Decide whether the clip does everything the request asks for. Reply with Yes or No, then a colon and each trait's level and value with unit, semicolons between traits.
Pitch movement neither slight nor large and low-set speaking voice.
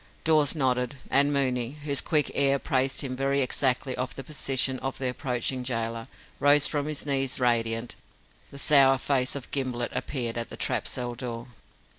No: narrow, 2.0 semitones; low, 130 Hz